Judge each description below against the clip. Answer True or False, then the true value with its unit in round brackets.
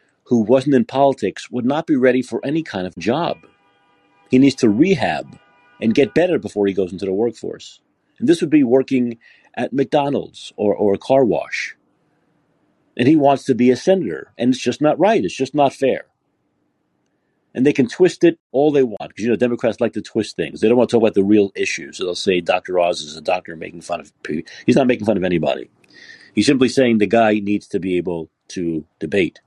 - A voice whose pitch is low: True (120 Hz)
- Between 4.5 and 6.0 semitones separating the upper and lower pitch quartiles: True (5.2 semitones)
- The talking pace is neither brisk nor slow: False (220 wpm)